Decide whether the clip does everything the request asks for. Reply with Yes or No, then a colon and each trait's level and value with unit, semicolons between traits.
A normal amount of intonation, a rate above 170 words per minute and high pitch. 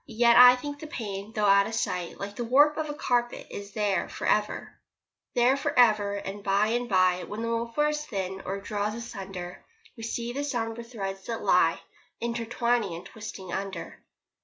Yes: average, 3.4 semitones; average, 185 wpm; high, 225 Hz